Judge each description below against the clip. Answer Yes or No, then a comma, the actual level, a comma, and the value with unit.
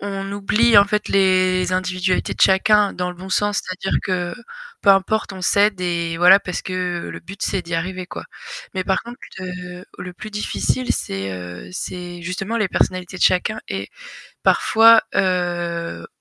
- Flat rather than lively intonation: Yes, narrow, 2.0 semitones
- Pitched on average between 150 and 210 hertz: Yes, medium, 185 Hz